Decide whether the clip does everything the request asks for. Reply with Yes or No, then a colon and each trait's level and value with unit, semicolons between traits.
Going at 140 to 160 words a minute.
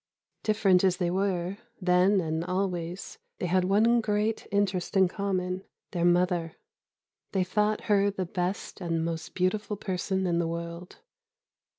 Yes: average, 145 wpm